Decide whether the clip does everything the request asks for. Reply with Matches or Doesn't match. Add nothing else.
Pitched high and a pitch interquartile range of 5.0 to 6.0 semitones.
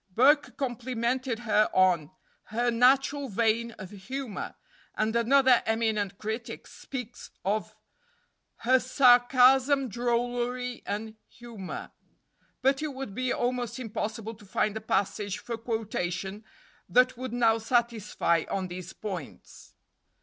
Doesn't match